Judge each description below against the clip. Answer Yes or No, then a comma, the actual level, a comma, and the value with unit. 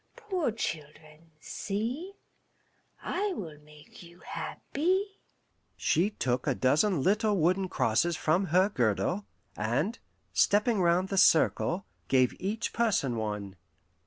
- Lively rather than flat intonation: Yes, wide, 6.2 semitones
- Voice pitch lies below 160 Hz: No, medium, 180 Hz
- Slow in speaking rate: Yes, slow, 115 wpm